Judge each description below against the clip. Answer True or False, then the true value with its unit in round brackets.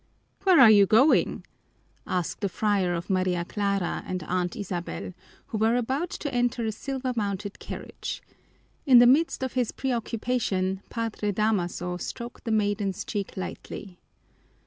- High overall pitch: True (210 Hz)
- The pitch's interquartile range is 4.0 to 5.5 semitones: True (4.5 semitones)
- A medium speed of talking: True (145 wpm)